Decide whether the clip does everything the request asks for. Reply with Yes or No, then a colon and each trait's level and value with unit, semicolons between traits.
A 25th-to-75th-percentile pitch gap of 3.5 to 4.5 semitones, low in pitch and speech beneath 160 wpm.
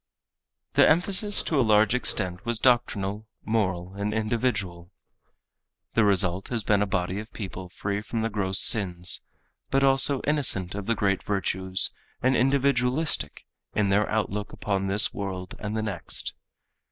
Yes: average, 3.8 semitones; low, 105 Hz; average, 150 wpm